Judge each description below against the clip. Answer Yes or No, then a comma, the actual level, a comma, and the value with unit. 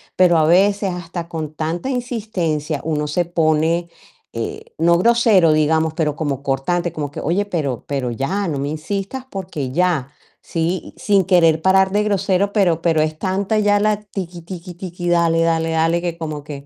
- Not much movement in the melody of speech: No, average, 3.6 semitones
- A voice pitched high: No, medium, 170 Hz